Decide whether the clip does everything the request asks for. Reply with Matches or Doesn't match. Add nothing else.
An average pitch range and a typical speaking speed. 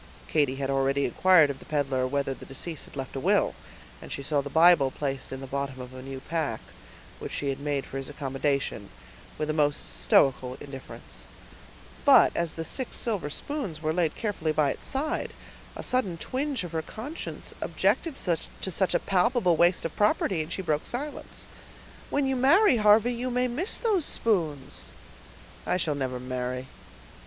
Doesn't match